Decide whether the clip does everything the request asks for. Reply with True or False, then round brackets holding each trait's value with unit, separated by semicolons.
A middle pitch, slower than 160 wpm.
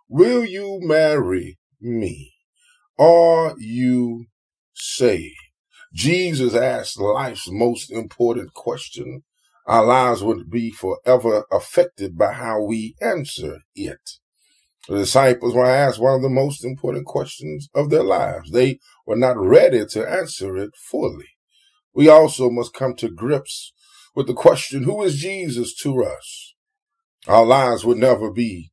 False (130 Hz; 135 wpm)